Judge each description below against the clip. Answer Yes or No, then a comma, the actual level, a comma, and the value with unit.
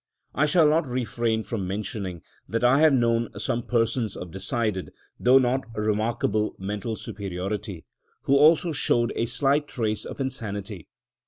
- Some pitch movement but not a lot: Yes, average, 4.0 semitones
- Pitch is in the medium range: No, low, 115 Hz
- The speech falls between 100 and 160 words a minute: Yes, average, 145 wpm